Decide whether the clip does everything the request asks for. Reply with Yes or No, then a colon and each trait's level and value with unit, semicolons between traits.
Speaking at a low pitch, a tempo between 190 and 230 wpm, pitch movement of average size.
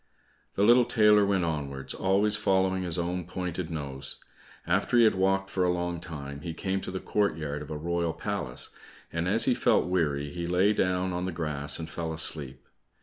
Yes: very low, 90 Hz; average, 195 wpm; average, 3.6 semitones